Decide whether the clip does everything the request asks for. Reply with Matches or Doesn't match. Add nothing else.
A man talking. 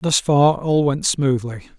Matches